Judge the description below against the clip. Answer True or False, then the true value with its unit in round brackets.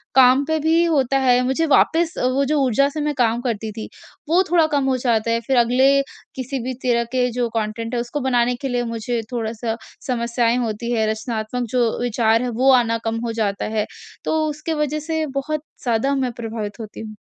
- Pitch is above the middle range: True (245 Hz)